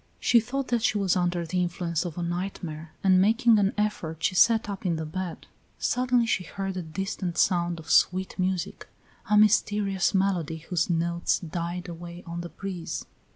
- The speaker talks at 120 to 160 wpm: No, average, 180 wpm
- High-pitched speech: No, medium, 180 Hz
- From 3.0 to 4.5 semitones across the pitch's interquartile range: No, narrow, 2.6 semitones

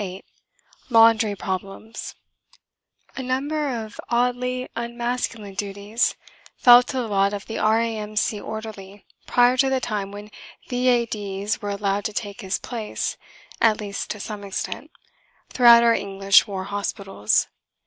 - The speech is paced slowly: Yes, slow, 130 wpm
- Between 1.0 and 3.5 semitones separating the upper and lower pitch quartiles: Yes, average, 3.0 semitones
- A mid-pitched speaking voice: No, high, 215 Hz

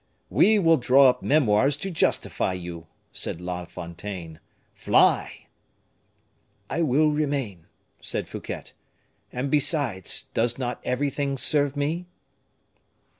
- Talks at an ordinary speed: No, slow, 110 wpm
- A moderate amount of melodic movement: No, wide, 7.5 semitones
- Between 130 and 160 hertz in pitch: Yes, low, 135 Hz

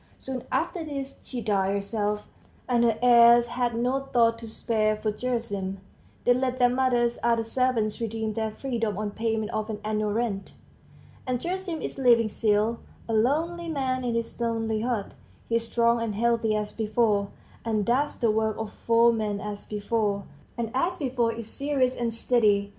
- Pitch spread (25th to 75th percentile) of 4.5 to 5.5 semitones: No, narrow, 2.6 semitones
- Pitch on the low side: No, high, 230 Hz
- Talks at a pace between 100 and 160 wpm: No, average, 175 wpm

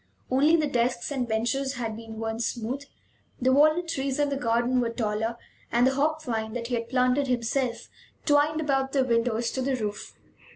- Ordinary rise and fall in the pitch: Yes, average, 3.0 semitones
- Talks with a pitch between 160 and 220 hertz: No, very high, 250 Hz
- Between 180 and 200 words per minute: Yes, average, 190 wpm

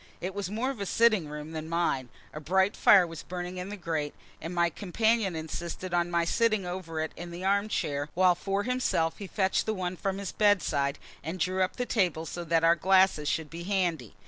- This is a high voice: No, medium, 180 Hz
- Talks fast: Yes, fast, 220 wpm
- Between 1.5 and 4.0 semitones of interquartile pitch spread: Yes, average, 3.2 semitones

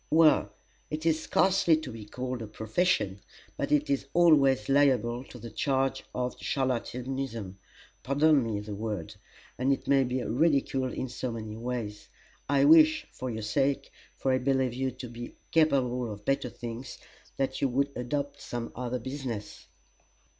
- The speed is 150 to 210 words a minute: Yes, average, 160 wpm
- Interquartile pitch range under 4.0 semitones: Yes, average, 3.0 semitones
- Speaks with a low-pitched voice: Yes, low, 130 Hz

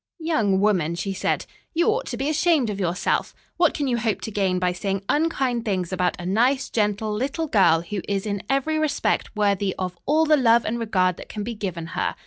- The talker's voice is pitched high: Yes, high, 215 Hz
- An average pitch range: No, wide, 6.2 semitones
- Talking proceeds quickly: Yes, fast, 215 wpm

